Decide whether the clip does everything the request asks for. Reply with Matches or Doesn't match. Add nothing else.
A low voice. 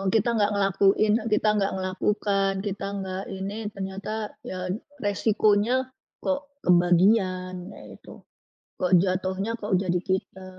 Doesn't match